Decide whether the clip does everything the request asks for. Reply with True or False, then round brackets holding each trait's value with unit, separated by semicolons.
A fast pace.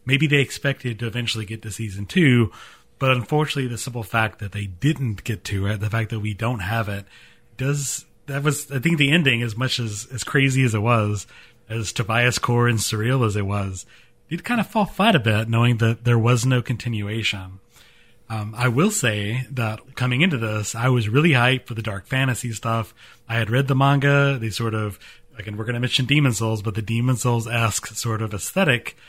True (210 wpm)